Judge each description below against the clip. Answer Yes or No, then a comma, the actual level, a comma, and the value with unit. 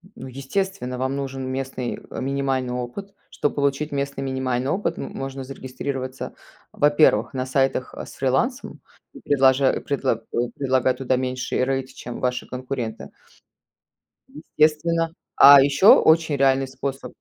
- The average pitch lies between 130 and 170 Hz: Yes, low, 135 Hz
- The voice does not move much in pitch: Yes, narrow, 1.5 semitones